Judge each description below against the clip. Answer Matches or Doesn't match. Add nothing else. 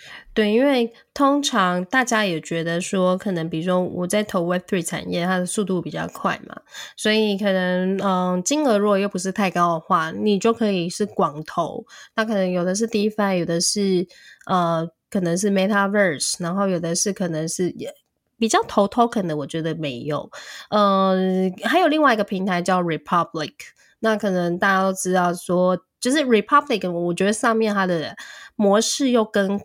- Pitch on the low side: Doesn't match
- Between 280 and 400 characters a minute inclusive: Matches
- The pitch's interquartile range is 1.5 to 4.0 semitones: Matches